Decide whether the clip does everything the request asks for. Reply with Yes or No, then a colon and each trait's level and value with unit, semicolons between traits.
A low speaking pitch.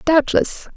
No: very high, 315 Hz